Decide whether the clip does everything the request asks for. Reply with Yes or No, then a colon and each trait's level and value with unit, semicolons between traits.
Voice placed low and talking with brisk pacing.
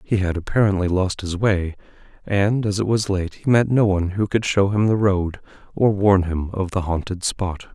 Yes: very low, 95 Hz; fast, 215 wpm